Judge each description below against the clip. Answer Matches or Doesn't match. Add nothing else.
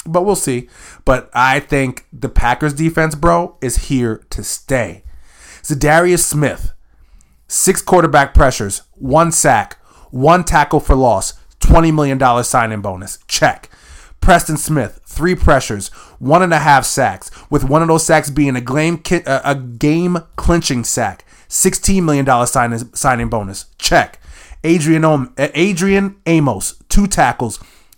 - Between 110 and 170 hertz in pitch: Matches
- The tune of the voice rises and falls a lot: Matches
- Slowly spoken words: Matches